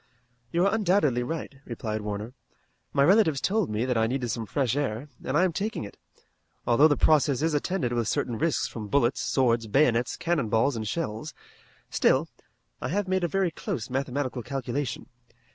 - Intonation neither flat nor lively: No, wide, 5.7 semitones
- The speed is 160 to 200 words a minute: Yes, average, 180 wpm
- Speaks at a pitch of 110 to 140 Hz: Yes, low, 135 Hz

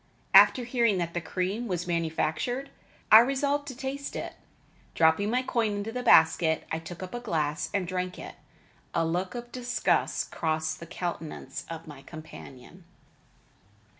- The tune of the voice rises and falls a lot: Yes, wide, 6.9 semitones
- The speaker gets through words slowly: No, average, 155 wpm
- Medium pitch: Yes, medium, 180 Hz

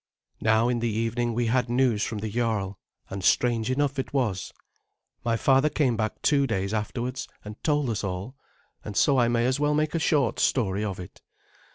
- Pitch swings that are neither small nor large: Yes, average, 3.6 semitones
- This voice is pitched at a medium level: No, low, 120 Hz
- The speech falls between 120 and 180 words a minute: No, average, 195 wpm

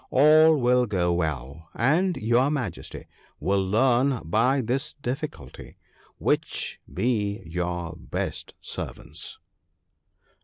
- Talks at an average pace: No, slow, 100 wpm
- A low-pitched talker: Yes, low, 115 Hz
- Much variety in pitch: Yes, wide, 7.4 semitones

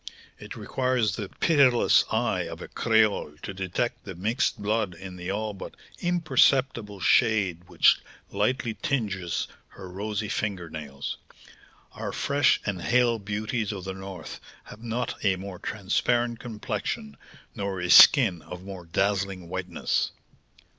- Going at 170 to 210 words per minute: No, slow, 135 wpm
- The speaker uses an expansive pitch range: No, average, 4.2 semitones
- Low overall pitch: Yes, low, 100 Hz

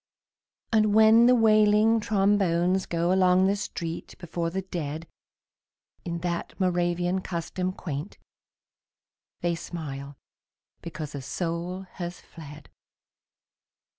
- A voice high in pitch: No, medium, 175 Hz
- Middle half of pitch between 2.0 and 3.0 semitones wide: Yes, narrow, 2.5 semitones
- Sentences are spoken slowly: Yes, slow, 105 wpm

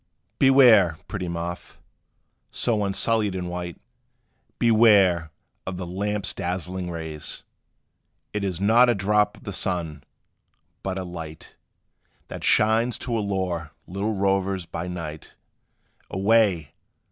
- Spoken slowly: Yes, slow, 115 wpm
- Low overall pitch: Yes, very low, 95 Hz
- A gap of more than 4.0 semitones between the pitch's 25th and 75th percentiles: No, average, 3.1 semitones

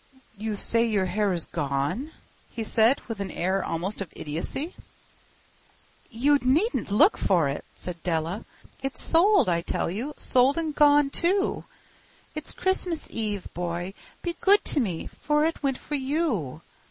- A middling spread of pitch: No, wide, 8.7 semitones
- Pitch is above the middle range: Yes, high, 225 Hz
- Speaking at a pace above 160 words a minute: No, average, 150 wpm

